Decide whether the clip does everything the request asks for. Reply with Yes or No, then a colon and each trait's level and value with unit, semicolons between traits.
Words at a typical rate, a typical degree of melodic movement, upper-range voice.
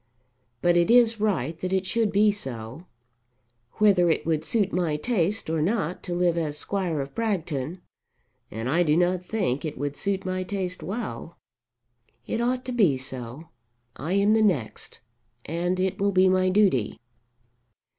No: average, 165 wpm; average, 4.6 semitones; medium, 180 Hz